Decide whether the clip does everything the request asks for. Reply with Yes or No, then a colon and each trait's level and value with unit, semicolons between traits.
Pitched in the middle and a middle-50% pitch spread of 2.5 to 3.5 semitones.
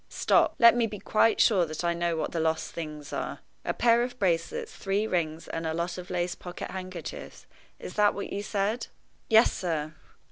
No: medium, 180 Hz; average, 4.0 semitones